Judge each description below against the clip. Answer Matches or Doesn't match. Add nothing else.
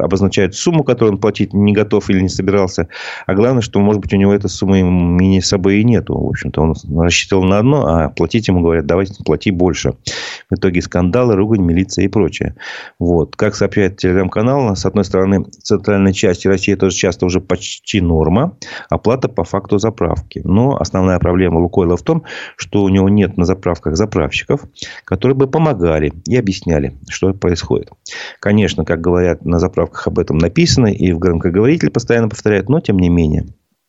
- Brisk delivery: Matches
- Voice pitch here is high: Doesn't match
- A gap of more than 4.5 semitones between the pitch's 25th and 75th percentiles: Doesn't match